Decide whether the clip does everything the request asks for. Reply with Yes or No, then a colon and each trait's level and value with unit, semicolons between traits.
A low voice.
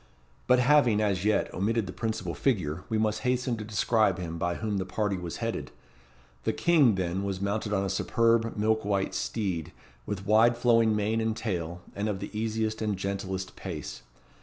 Yes: low, 105 Hz